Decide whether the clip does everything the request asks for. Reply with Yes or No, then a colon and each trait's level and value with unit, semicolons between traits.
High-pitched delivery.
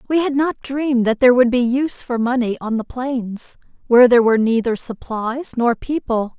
Yes: high, 245 Hz